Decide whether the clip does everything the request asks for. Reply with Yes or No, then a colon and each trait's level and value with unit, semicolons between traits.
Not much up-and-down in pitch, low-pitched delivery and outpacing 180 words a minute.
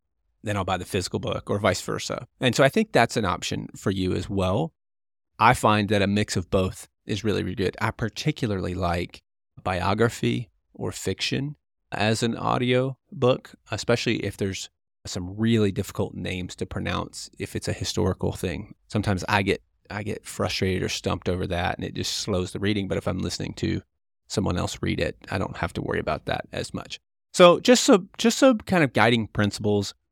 No: average, 4.0 semitones; low, 105 Hz; average, 195 wpm